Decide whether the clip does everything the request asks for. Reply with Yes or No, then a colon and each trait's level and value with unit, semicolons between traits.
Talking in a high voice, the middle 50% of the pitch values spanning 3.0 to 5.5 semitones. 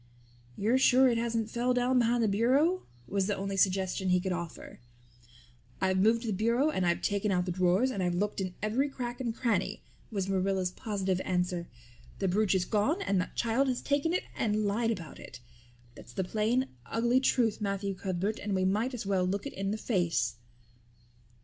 Yes: high, 205 Hz; average, 4.1 semitones